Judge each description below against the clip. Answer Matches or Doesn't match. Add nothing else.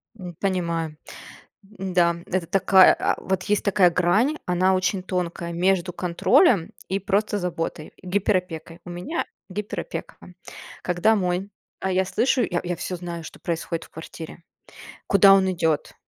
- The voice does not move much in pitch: Matches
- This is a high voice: Doesn't match